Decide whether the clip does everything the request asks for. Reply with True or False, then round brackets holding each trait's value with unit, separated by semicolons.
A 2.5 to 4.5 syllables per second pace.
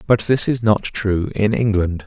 True (4.2 syllables/s)